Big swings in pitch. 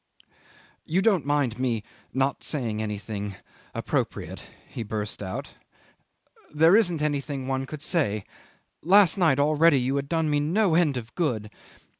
Yes: wide, 5.9 semitones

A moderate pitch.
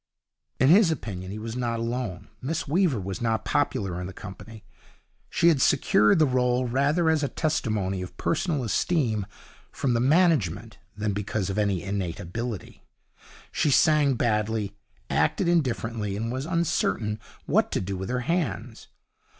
No: low, 115 Hz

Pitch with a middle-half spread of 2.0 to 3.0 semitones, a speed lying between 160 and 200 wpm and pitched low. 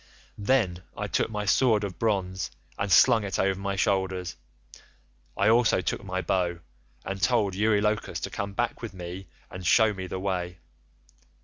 Yes: narrow, 2.4 semitones; average, 165 wpm; low, 100 Hz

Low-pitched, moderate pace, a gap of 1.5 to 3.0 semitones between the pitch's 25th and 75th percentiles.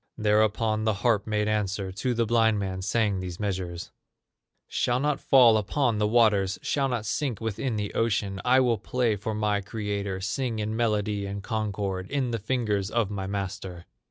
Yes: low, 105 Hz; average, 175 wpm; average, 2.7 semitones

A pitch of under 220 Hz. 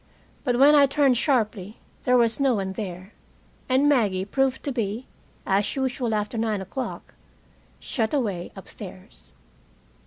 No: high, 235 Hz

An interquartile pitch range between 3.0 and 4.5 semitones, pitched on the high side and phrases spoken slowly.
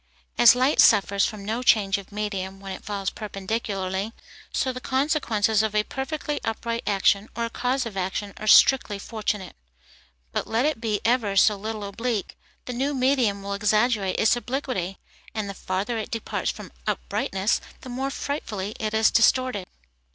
No: average, 3.7 semitones; high, 215 Hz; average, 165 wpm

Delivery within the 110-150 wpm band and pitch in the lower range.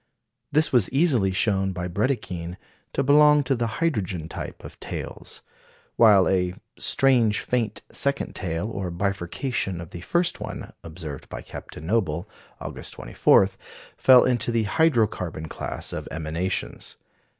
Yes: average, 140 wpm; low, 100 Hz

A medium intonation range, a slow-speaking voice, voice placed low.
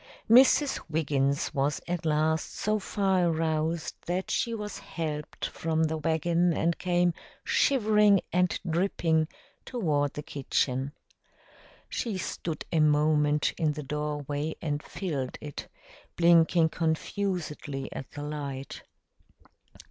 No: average, 3.0 semitones; slow, 115 wpm; medium, 160 Hz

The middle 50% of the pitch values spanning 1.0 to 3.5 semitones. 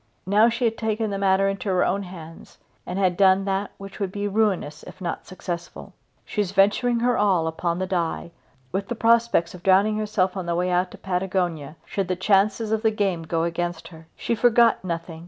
Yes: average, 3.1 semitones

